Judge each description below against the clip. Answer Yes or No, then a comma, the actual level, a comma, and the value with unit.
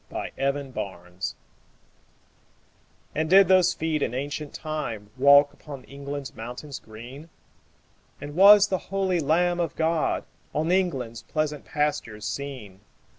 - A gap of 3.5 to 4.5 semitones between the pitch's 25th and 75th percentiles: Yes, average, 4.2 semitones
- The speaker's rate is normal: No, slow, 125 wpm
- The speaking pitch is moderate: Yes, medium, 145 Hz